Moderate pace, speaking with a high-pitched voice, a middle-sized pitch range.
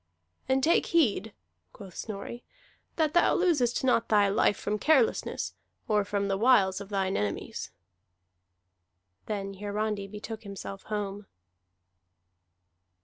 No: slow, 115 wpm; high, 210 Hz; average, 3.4 semitones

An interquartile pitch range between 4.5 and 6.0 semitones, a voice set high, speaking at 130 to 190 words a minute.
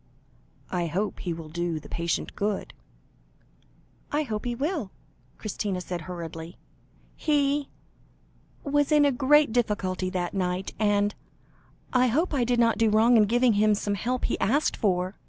Yes: wide, 5.6 semitones; high, 215 Hz; average, 155 wpm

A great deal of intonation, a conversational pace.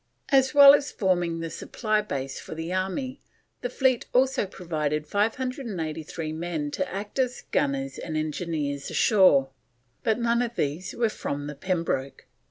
Yes: wide, 7.4 semitones; average, 150 wpm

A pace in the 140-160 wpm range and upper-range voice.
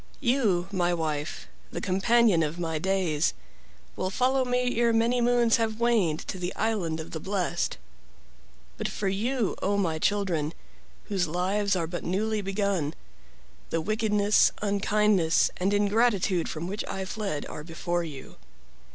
Yes: average, 145 wpm; high, 195 Hz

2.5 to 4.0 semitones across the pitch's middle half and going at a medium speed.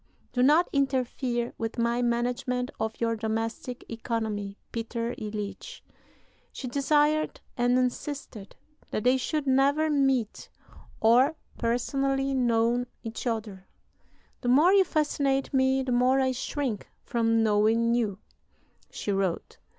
No: average, 3.0 semitones; slow, 120 wpm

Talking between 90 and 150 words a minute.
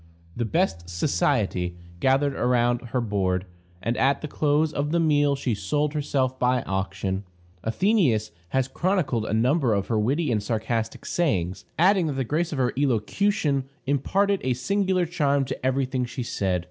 No: average, 165 wpm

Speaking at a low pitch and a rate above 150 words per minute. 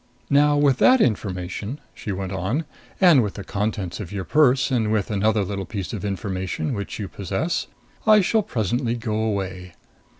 Yes: low, 105 Hz; average, 170 wpm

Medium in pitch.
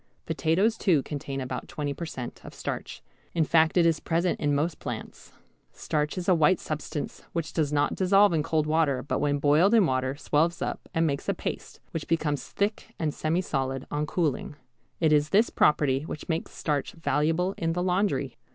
Yes: medium, 155 Hz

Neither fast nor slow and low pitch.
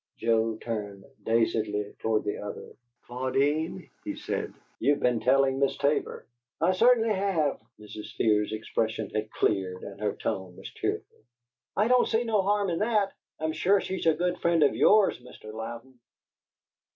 Yes: average, 155 wpm; low, 130 Hz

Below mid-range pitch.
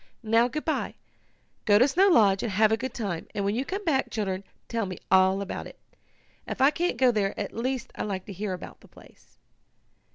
No: high, 220 Hz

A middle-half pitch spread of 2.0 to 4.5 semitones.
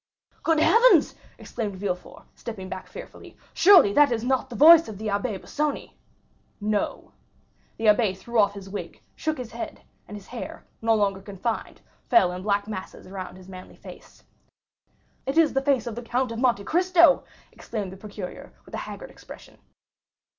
No: average, 5.2 semitones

